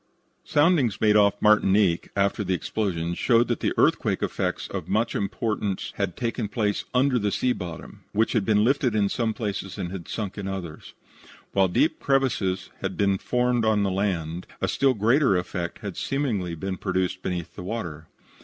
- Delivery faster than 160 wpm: Yes, average, 175 wpm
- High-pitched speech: No, low, 100 Hz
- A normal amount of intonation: Yes, average, 3.7 semitones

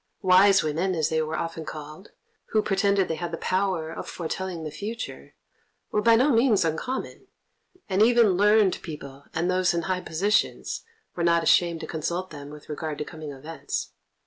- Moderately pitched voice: Yes, medium, 175 Hz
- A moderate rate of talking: Yes, average, 175 wpm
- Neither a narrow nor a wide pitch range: Yes, average, 3.9 semitones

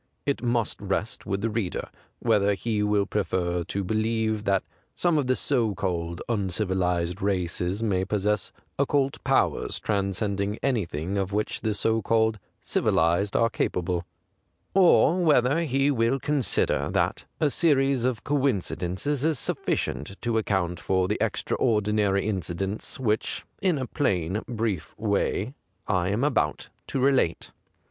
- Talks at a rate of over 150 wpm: No, average, 140 wpm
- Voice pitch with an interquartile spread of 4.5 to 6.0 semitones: Yes, average, 4.8 semitones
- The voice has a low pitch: Yes, low, 105 Hz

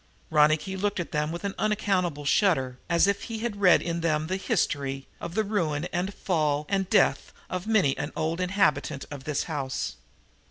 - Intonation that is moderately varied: Yes, average, 4.8 semitones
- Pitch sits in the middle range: Yes, medium, 170 Hz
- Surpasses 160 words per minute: Yes, average, 175 wpm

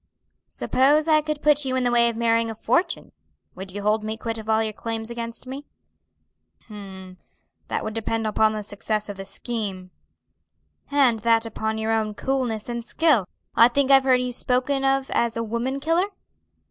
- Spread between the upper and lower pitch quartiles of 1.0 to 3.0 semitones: No, average, 3.4 semitones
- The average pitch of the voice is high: Yes, high, 230 Hz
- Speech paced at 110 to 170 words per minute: No, average, 185 wpm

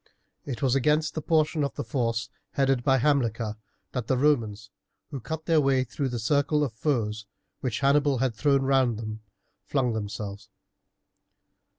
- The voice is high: No, low, 130 Hz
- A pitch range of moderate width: Yes, average, 3.9 semitones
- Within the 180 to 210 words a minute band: No, average, 160 wpm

